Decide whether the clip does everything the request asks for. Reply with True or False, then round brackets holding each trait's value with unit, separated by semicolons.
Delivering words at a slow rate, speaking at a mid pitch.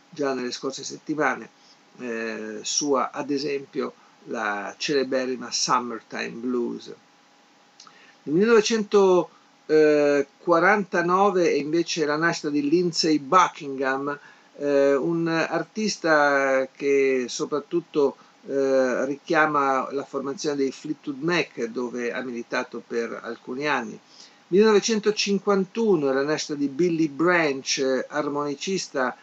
True (95 wpm; 145 Hz)